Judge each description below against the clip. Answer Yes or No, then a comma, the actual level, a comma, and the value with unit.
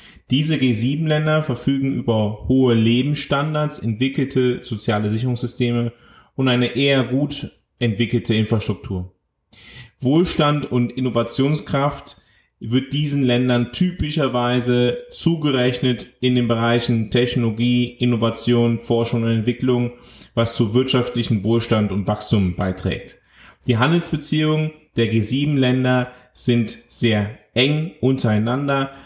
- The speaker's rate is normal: No, slow, 95 wpm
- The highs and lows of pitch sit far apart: No, average, 2.7 semitones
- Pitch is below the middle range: Yes, low, 125 Hz